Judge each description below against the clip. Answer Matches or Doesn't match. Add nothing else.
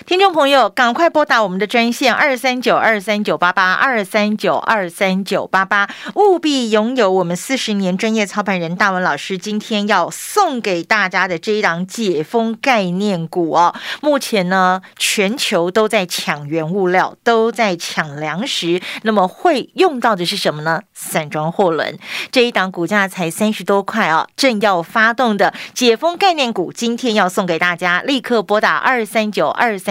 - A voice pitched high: Matches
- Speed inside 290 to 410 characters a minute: Doesn't match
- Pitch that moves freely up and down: Doesn't match